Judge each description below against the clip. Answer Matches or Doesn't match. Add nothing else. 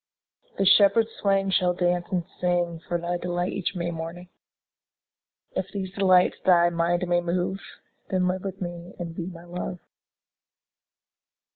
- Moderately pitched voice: Matches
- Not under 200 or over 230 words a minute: Doesn't match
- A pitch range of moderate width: Doesn't match